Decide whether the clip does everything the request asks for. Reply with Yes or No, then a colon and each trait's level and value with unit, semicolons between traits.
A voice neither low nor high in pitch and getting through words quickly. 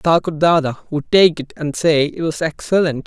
No: medium, 160 Hz; average, 195 wpm